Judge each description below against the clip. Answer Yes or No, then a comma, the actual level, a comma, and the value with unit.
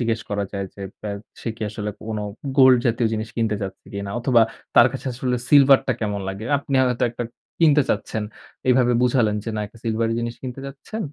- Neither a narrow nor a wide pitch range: Yes, average, 3.2 semitones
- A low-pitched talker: Yes, low, 115 Hz